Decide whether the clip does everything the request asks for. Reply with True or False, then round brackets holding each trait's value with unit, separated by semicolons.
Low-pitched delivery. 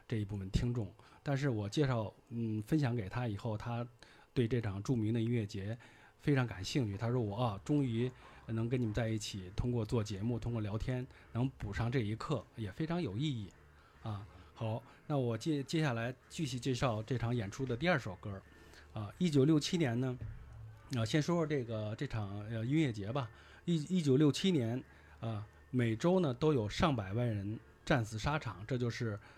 True (120 Hz)